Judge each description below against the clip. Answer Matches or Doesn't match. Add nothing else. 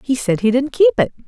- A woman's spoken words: Matches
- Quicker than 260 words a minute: Matches